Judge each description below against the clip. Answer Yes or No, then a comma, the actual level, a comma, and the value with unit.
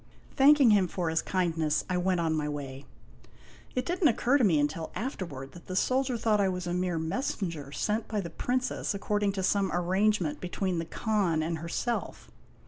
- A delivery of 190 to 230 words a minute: Yes, average, 195 wpm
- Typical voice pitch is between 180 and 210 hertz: Yes, medium, 185 Hz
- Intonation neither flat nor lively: Yes, average, 4.7 semitones